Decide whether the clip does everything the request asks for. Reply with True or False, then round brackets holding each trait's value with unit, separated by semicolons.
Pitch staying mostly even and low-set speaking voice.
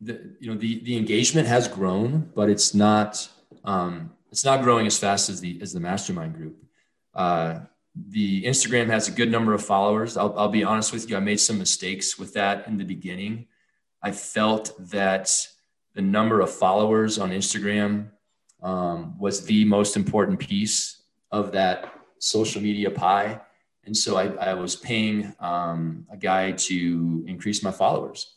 True (2.3 semitones; 105 Hz)